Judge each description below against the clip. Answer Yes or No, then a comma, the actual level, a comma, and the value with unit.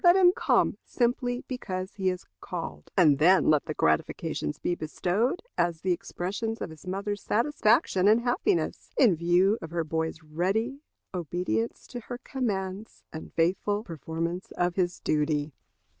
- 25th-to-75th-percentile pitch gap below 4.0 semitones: No, wide, 5.5 semitones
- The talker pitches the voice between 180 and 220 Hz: Yes, medium, 185 Hz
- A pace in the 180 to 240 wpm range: No, average, 150 wpm